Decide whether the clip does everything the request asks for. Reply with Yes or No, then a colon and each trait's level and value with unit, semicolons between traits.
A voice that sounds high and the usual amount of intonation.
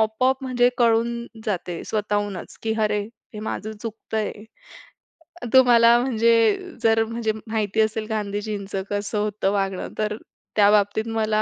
No: high, 215 Hz; narrow, 1.7 semitones